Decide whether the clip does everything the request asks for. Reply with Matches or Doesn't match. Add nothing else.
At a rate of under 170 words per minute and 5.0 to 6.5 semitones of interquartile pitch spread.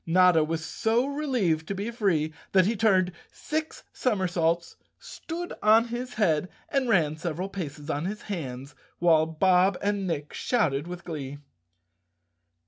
Matches